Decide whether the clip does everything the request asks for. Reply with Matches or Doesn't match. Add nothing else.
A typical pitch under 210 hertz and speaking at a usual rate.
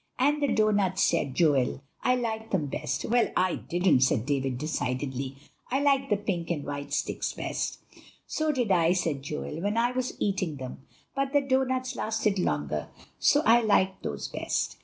Matches